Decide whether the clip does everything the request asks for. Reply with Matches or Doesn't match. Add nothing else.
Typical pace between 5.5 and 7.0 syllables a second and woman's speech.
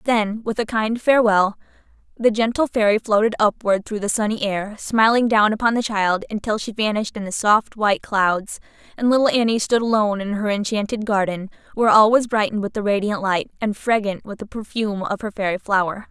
Matches